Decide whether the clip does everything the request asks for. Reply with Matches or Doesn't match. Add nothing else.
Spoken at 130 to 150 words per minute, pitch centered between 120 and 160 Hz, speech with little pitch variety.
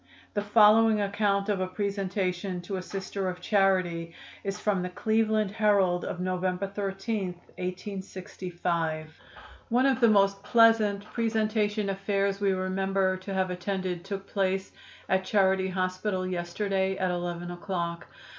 Doesn't match